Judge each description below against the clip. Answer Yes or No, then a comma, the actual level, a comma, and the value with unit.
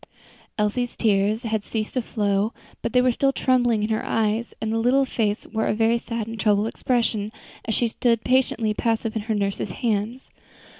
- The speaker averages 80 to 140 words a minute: No, average, 190 wpm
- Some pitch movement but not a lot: No, narrow, 2.2 semitones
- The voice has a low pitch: No, high, 225 Hz